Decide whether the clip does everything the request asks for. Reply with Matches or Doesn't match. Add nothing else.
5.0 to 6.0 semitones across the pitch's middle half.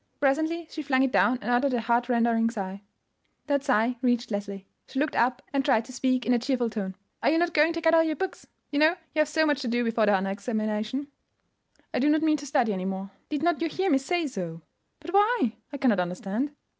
Matches